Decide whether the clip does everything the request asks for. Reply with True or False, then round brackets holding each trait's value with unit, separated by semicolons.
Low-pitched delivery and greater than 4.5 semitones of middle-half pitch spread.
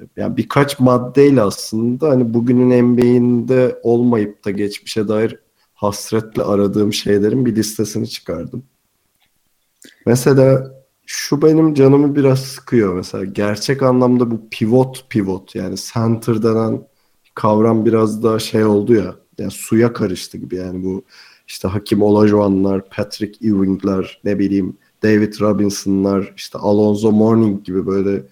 False (110 Hz; 3.3 semitones)